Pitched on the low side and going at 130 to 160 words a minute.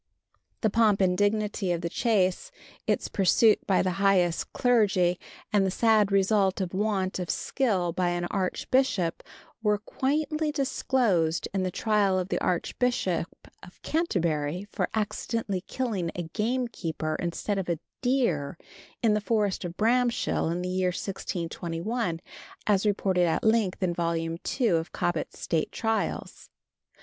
No: high, 195 Hz; average, 145 wpm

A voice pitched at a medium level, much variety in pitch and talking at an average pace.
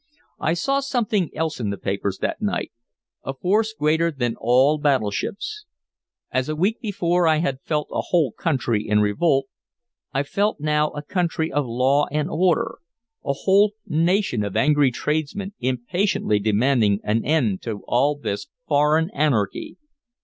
Yes: medium, 150 Hz; wide, 5.9 semitones; average, 150 wpm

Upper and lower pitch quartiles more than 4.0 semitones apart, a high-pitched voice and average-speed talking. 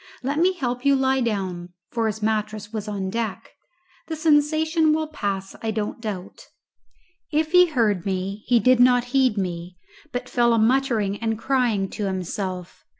Yes: average, 5.0 semitones; high, 225 Hz; average, 165 wpm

